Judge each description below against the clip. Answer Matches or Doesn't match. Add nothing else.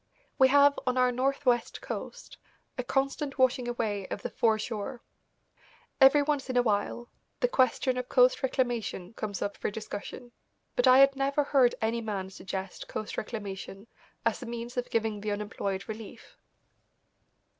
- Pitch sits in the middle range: Doesn't match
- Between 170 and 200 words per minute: Doesn't match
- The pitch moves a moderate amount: Matches